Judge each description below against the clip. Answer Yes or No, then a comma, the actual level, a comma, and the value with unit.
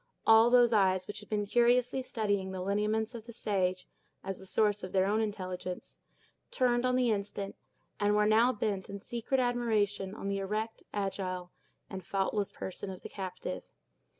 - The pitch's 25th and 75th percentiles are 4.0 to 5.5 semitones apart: No, average, 2.7 semitones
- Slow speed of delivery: No, average, 175 wpm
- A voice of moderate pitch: No, high, 205 Hz